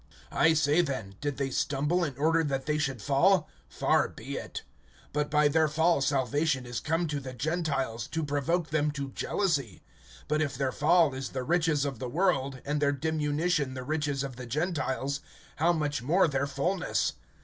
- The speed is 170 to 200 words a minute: Yes, average, 180 wpm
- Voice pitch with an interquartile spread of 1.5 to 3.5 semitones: Yes, average, 3.0 semitones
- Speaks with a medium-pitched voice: Yes, medium, 145 Hz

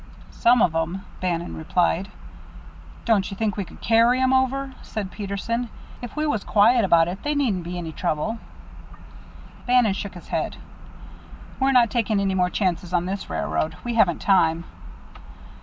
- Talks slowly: No, average, 160 wpm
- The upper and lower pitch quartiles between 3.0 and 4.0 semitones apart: No, average, 5.1 semitones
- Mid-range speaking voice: No, high, 200 Hz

